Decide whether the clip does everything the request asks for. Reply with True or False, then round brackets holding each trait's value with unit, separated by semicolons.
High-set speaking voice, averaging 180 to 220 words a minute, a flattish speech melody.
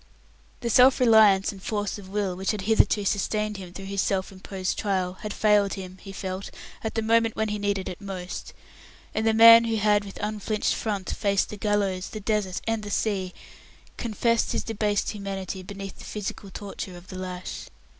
True (205 Hz; 190 wpm; 2.1 semitones)